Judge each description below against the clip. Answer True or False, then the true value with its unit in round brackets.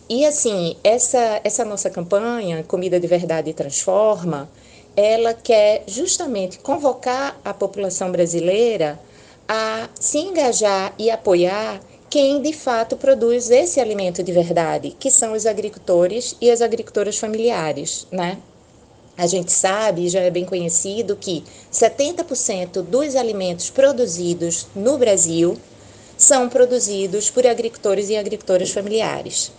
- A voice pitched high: True (210 Hz)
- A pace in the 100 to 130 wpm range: True (120 wpm)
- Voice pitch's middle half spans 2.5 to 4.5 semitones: False (4.9 semitones)